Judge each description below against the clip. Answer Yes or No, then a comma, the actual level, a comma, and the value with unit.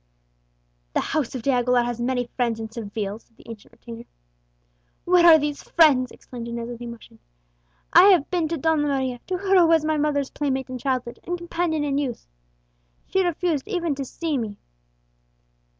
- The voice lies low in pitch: No, very high, 275 Hz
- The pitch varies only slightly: No, average, 5.2 semitones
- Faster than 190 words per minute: No, average, 180 wpm